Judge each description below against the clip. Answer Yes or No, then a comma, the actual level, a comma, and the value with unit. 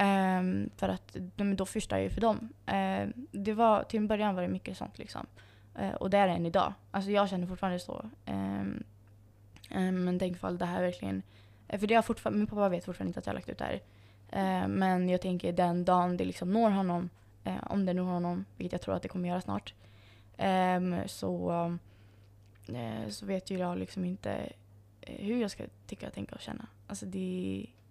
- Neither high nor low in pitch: Yes, medium, 175 Hz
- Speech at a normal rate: No, fast, 210 wpm